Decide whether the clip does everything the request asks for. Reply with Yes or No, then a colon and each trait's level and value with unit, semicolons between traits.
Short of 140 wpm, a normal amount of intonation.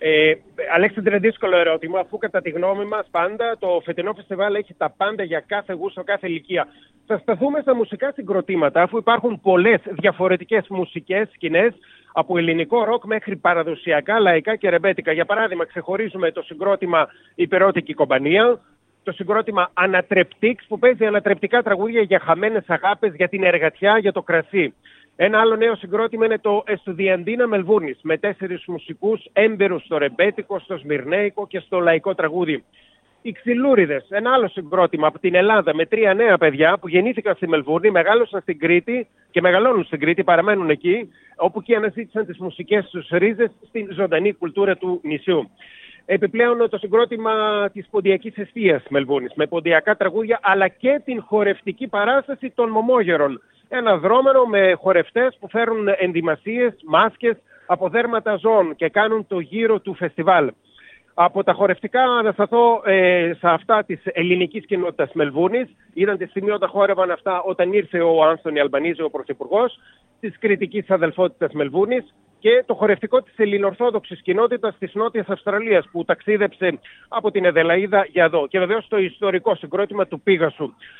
No: average, 155 wpm; average, 3.6 semitones